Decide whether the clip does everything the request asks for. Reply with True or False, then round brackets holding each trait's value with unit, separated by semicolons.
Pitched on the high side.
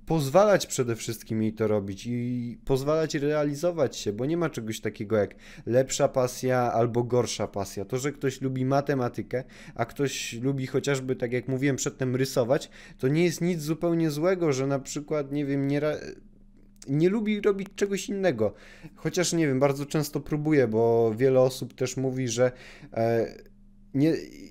False (135 Hz)